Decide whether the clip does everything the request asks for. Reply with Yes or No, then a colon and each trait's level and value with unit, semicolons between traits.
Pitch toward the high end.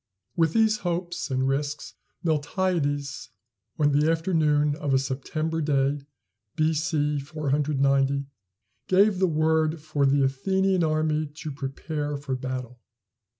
No: medium, 150 Hz